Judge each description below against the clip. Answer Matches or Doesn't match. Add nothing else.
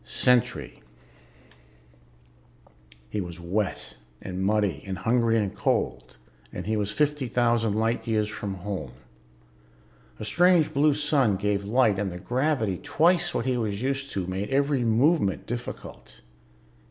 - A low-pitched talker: Matches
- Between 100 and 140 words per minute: Matches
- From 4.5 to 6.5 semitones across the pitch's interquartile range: Matches